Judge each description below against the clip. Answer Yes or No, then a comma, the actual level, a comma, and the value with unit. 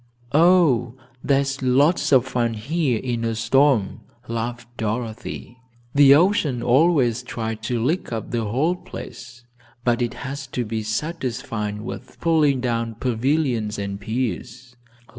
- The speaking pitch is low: Yes, low, 125 Hz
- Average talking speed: No, slow, 130 wpm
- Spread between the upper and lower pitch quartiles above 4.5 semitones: No, average, 3.5 semitones